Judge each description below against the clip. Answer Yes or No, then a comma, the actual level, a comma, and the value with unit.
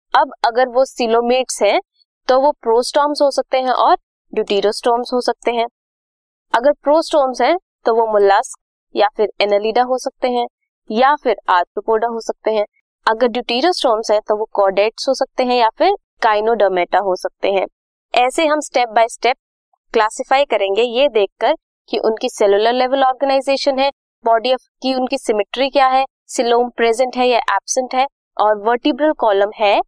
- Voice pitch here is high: Yes, high, 245 Hz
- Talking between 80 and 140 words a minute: No, average, 165 wpm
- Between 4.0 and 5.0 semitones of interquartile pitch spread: No, average, 3.6 semitones